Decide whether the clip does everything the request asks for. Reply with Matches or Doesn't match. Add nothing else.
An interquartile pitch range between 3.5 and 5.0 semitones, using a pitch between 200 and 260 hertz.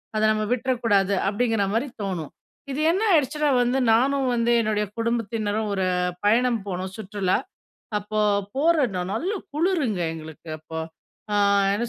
Matches